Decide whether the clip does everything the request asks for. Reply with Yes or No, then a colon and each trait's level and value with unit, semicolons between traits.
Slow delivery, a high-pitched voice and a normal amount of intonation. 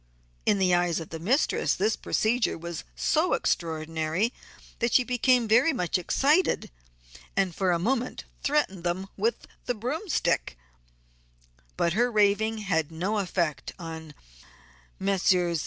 No: slow, 130 wpm; high, 195 Hz; wide, 5.8 semitones